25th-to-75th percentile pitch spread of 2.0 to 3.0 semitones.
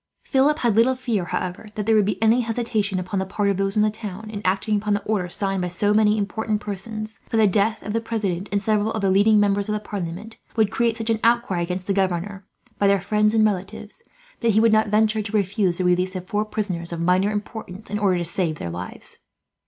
Yes: narrow, 2.4 semitones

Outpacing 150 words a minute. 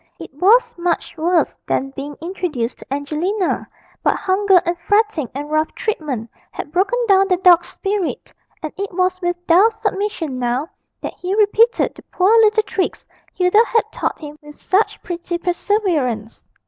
Yes: average, 160 wpm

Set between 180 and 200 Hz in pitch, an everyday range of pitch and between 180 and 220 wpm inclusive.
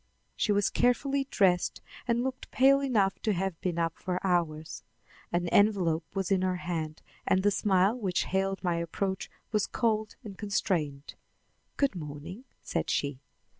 No: high, 190 Hz; average, 3.8 semitones; average, 155 wpm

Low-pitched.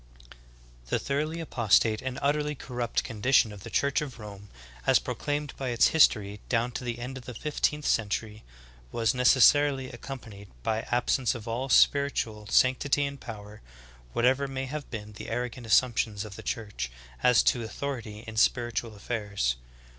Yes: low, 120 Hz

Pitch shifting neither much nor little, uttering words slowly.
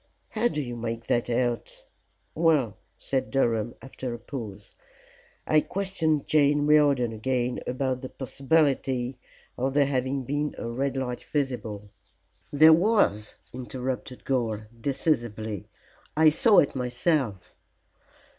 Yes: average, 3.7 semitones; slow, 120 wpm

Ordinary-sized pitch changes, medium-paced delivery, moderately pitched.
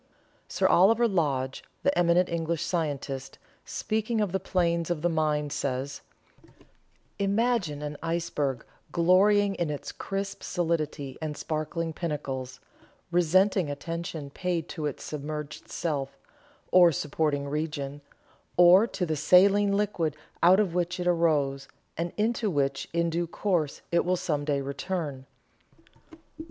No: average, 3.8 semitones; slow, 130 wpm; medium, 165 Hz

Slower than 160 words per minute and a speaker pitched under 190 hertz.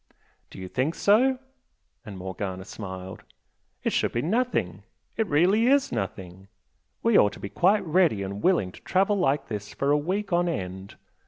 No: average, 170 wpm; medium, 140 Hz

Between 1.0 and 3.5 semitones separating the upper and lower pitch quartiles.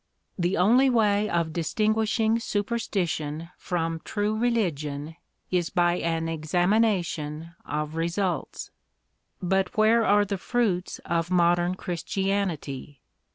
No: average, 4.2 semitones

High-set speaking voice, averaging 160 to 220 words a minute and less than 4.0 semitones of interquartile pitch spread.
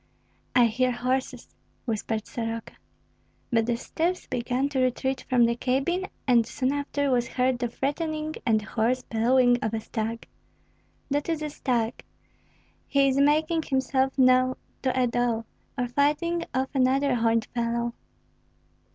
No: very high, 255 Hz; average, 140 wpm; average, 2.8 semitones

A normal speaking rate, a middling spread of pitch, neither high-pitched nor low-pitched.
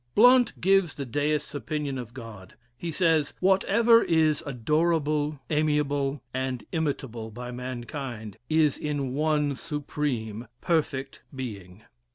No: slow, 115 wpm; average, 3.9 semitones; medium, 145 Hz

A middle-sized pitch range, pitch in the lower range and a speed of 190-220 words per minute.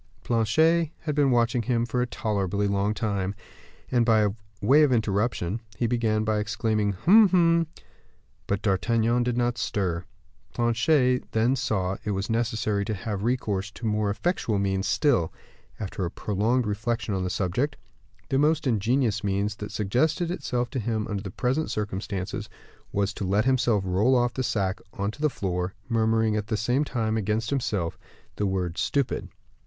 No: average, 3.6 semitones; low, 110 Hz; average, 170 wpm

